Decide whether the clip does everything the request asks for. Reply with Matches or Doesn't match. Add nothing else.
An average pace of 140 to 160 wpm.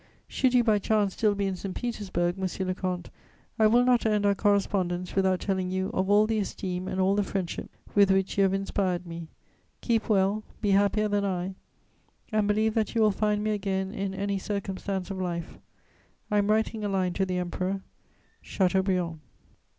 Doesn't match